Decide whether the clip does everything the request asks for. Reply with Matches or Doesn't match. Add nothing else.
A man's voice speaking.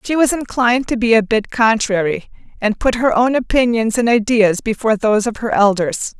Doesn't match